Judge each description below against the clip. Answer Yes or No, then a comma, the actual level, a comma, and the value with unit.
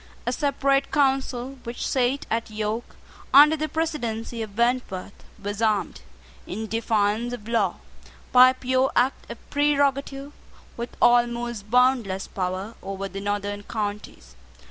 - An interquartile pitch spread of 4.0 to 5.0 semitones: Yes, average, 4.3 semitones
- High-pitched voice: Yes, high, 235 Hz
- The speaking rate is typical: No, slow, 130 wpm